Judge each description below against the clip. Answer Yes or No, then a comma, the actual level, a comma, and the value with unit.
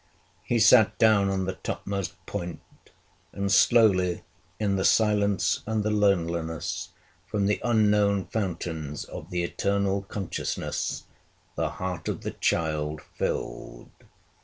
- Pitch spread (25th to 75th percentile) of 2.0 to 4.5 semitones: Yes, average, 3.2 semitones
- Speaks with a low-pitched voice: Yes, low, 100 Hz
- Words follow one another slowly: Yes, slow, 120 wpm